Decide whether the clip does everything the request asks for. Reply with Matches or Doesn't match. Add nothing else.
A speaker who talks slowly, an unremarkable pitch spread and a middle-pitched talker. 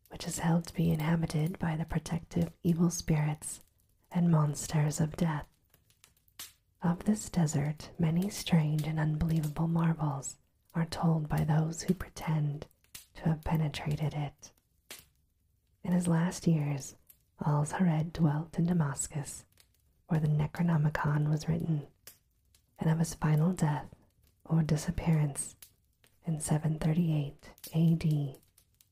Doesn't match